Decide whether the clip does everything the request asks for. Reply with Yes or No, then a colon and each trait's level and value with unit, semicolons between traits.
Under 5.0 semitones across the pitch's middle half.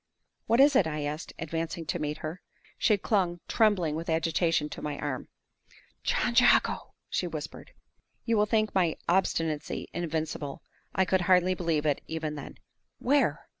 Yes: average, 3.5 semitones